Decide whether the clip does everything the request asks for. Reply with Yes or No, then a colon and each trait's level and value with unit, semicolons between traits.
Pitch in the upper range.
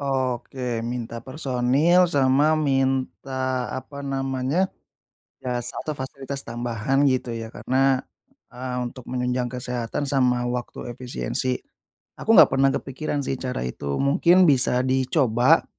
No: low, 130 Hz